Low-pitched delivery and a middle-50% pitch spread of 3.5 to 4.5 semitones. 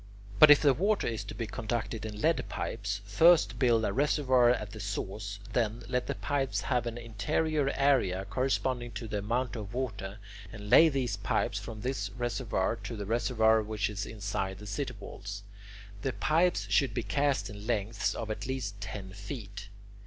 Yes: low, 115 Hz; average, 4.1 semitones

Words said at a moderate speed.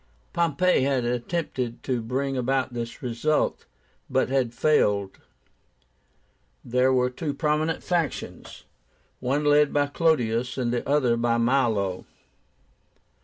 No: slow, 110 wpm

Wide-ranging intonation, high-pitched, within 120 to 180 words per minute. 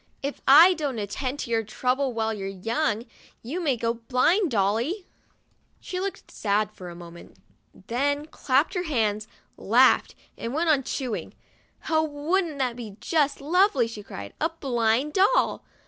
Yes: wide, 5.9 semitones; very high, 260 Hz; average, 170 wpm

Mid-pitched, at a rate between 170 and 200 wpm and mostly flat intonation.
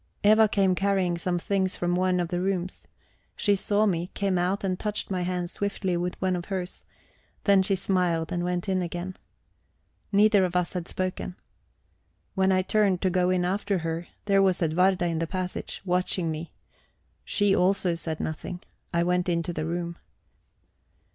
Yes: medium, 180 Hz; average, 175 wpm; narrow, 1.8 semitones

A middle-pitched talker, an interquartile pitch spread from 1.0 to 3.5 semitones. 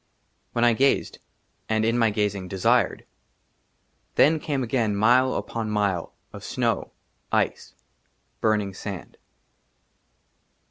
No: low, 110 Hz; average, 2.9 semitones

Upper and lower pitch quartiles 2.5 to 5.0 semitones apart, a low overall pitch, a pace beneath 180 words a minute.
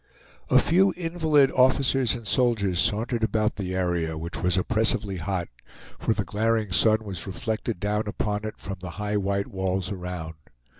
Yes: average, 3.6 semitones; low, 105 Hz; average, 160 wpm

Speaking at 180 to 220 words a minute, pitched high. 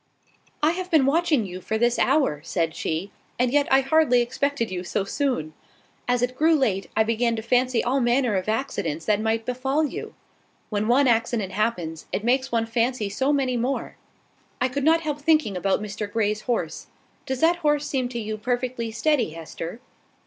Yes: average, 185 wpm; high, 240 Hz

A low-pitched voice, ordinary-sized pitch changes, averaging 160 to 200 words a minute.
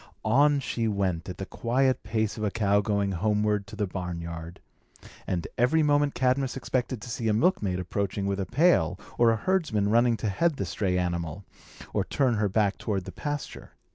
Yes: low, 105 Hz; average, 4.7 semitones; average, 190 wpm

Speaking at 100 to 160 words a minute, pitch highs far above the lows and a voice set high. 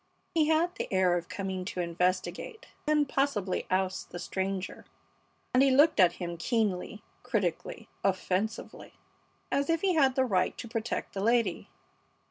Yes: average, 150 wpm; wide, 6.6 semitones; high, 205 Hz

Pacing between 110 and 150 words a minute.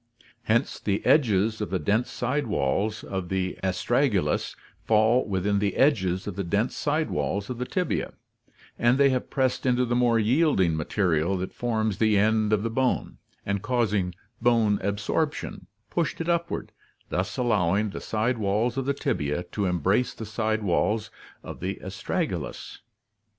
No: average, 160 wpm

